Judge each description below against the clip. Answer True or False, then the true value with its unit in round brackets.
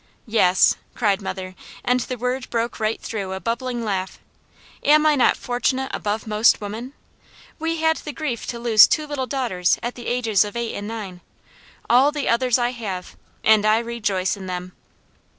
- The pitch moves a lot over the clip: False (3.6 semitones)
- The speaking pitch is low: False (235 Hz)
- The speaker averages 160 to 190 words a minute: True (175 wpm)